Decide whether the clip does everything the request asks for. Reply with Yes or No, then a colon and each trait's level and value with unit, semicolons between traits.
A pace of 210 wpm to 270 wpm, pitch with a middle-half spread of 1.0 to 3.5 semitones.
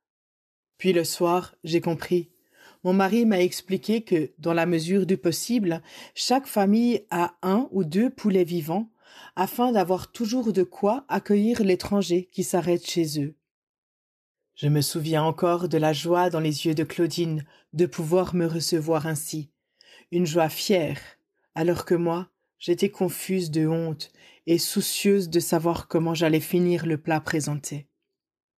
No: average, 150 wpm; average, 2.8 semitones